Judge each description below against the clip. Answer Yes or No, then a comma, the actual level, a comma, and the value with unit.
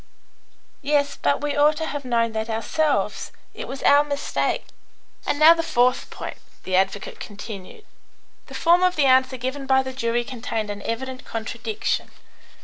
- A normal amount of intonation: Yes, average, 4.3 semitones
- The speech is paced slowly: No, average, 160 wpm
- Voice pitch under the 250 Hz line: No, very high, 260 Hz